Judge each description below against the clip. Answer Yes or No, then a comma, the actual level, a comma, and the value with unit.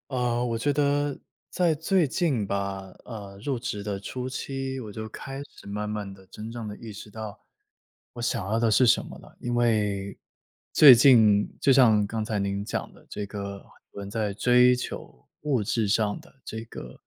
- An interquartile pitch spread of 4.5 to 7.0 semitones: No, average, 3.7 semitones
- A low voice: Yes, low, 110 Hz